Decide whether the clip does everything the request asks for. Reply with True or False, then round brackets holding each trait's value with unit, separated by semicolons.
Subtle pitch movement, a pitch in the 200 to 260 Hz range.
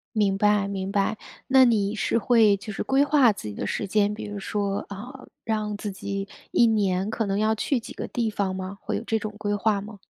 True (1.9 semitones; 210 Hz)